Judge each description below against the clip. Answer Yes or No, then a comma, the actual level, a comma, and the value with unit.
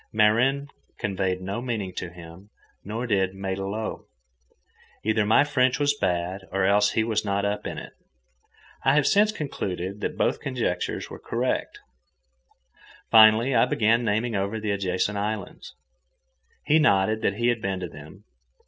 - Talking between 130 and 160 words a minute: Yes, average, 150 wpm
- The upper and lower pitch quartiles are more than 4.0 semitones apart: No, average, 3.5 semitones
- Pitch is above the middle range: No, low, 105 Hz